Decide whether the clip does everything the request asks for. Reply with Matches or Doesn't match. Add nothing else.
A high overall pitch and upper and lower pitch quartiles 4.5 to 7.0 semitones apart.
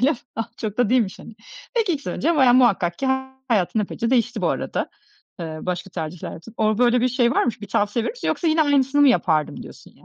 Matches